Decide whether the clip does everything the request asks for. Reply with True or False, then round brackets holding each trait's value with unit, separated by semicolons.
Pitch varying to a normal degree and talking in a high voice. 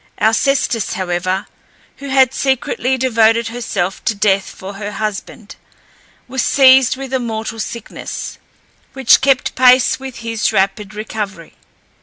True (4.1 semitones; 225 Hz)